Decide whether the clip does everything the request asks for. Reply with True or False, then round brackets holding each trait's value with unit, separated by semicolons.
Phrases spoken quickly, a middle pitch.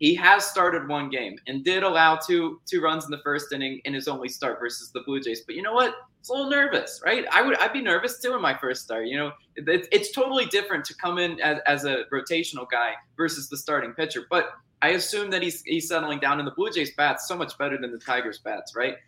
True (255 wpm; 160 Hz)